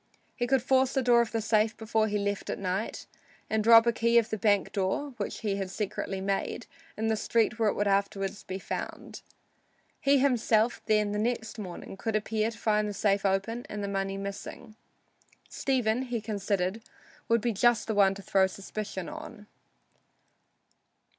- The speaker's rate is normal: Yes, average, 180 wpm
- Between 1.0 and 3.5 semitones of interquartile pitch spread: Yes, average, 2.7 semitones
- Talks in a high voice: Yes, high, 215 Hz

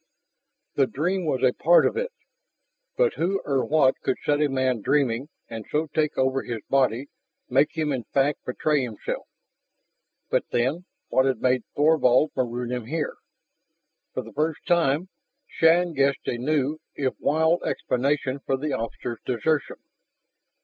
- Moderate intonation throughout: Yes, average, 3.4 semitones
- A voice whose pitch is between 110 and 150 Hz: Yes, medium, 140 Hz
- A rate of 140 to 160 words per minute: Yes, average, 150 wpm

